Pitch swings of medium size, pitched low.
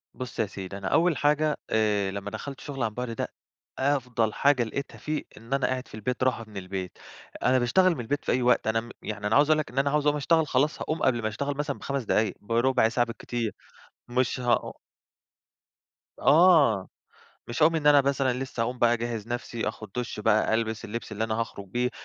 Yes: average, 4.2 semitones; low, 125 Hz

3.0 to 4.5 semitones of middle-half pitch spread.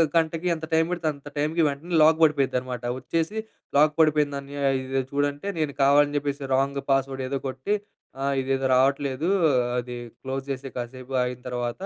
No: narrow, 2.5 semitones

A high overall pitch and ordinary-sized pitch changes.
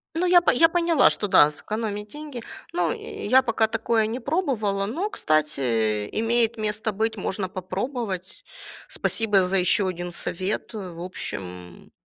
Yes: high, 210 Hz; average, 4.6 semitones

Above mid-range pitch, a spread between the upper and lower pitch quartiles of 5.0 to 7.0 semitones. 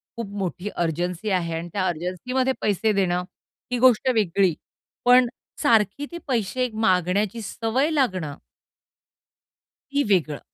Yes: high, 200 Hz; wide, 5.4 semitones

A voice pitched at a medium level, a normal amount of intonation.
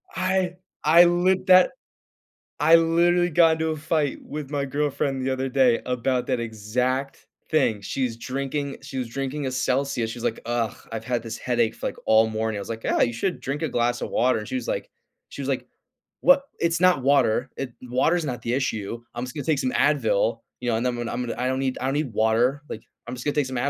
No: low, 130 Hz; average, 4.0 semitones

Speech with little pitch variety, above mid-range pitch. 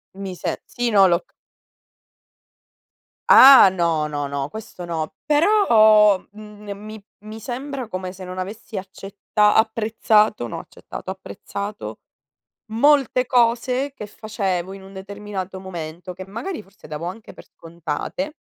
No: average, 3.4 semitones; high, 205 Hz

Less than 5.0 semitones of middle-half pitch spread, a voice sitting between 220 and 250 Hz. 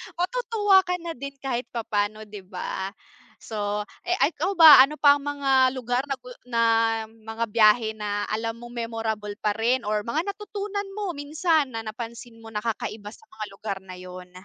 No: average, 5.3 semitones; high, 235 Hz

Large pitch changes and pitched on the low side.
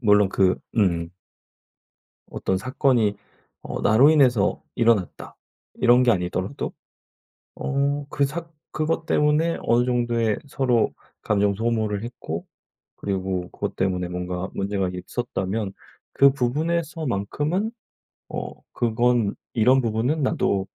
Yes: wide, 5.7 semitones; low, 115 Hz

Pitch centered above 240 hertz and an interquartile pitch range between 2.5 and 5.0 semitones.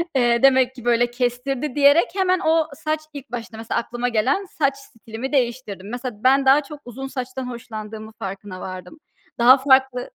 Yes: very high, 250 Hz; average, 2.8 semitones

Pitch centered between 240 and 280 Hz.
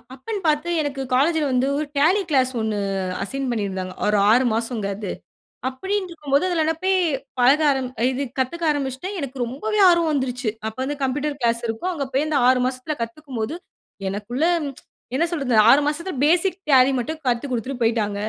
Yes: very high, 270 Hz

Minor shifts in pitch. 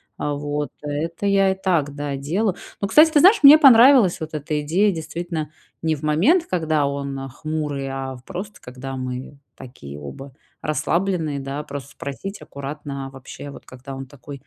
No: average, 4.8 semitones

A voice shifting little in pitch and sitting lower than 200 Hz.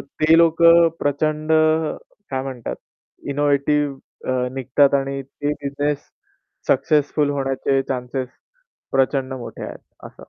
Yes: narrow, 1.8 semitones; medium, 140 Hz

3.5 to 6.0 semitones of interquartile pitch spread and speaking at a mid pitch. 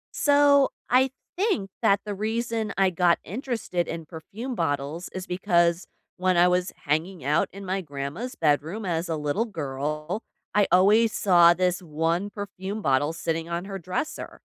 Yes: average, 4.1 semitones; medium, 180 Hz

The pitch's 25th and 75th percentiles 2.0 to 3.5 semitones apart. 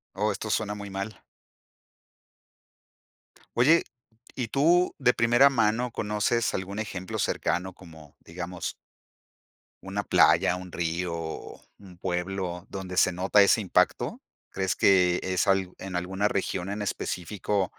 Yes: average, 2.8 semitones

